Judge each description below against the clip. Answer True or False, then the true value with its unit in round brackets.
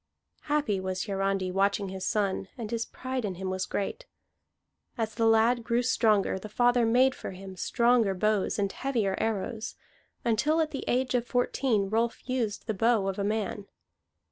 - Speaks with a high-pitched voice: True (220 Hz)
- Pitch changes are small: False (3.7 semitones)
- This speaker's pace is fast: False (170 wpm)